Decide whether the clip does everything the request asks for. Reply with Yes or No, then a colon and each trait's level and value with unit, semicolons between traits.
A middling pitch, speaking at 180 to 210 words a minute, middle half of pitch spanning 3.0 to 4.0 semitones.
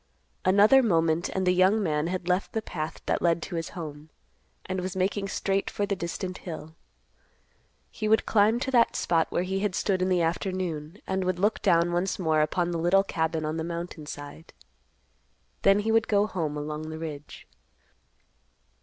Yes: medium, 180 Hz; average, 185 wpm; average, 3.3 semitones